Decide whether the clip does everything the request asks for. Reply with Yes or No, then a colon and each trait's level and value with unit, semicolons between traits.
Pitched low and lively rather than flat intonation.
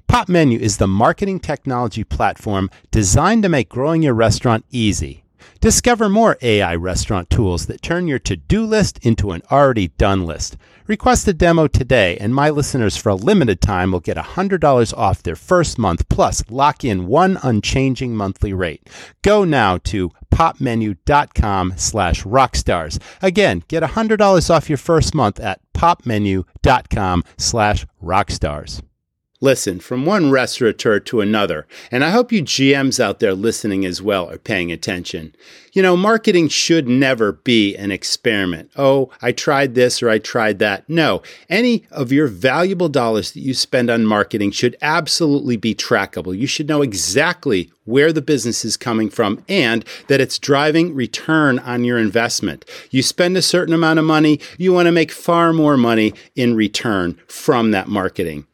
Yes: low, 120 Hz; wide, 7.9 semitones